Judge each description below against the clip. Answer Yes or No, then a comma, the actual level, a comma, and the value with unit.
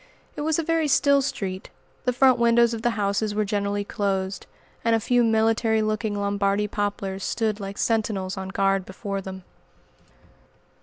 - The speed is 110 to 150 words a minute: No, average, 160 wpm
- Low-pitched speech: No, high, 210 Hz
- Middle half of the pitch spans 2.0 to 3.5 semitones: Yes, average, 2.8 semitones